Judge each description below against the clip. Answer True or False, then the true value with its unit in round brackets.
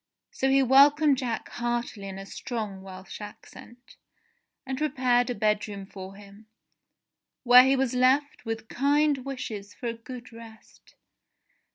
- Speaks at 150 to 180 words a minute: False (140 wpm)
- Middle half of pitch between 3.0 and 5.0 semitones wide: True (4.0 semitones)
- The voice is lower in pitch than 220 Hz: False (240 Hz)